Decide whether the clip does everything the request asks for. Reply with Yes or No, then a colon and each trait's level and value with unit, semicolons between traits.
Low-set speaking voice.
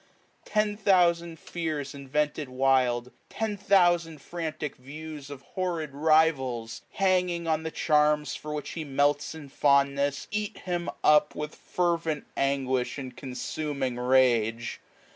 No: medium, 150 Hz